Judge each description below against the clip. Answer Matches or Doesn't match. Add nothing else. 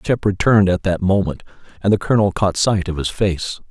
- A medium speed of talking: Doesn't match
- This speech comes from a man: Matches